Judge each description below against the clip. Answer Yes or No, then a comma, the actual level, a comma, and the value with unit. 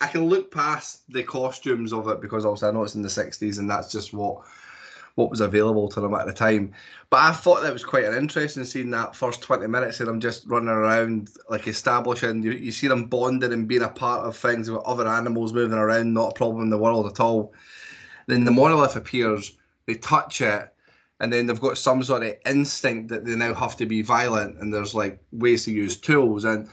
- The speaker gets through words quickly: Yes, fast, 230 wpm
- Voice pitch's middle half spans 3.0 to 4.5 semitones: No, narrow, 2.5 semitones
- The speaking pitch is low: Yes, low, 115 Hz